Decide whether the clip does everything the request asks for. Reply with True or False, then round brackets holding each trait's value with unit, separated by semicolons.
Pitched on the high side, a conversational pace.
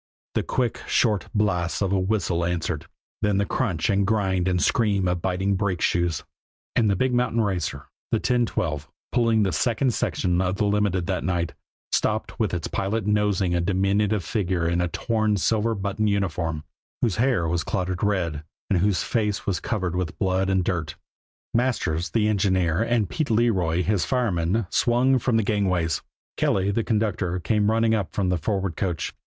False (95 Hz; 175 wpm)